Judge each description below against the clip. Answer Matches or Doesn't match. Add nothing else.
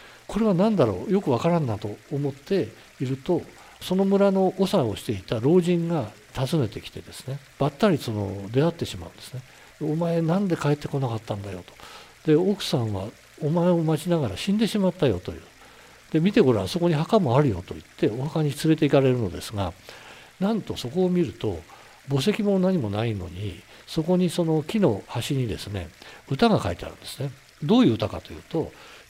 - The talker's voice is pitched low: Doesn't match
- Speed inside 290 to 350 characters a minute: Doesn't match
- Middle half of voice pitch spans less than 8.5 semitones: Matches